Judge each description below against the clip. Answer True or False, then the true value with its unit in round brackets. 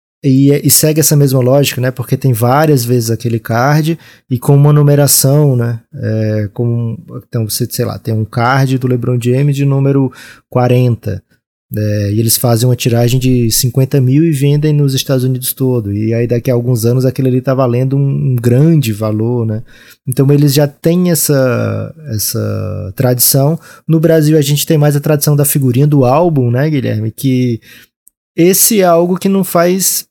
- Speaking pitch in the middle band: False (130 Hz)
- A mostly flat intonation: False (3.5 semitones)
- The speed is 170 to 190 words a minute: True (180 wpm)